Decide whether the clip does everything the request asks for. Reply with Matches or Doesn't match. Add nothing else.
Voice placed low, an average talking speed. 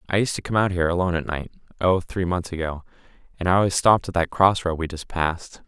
Doesn't match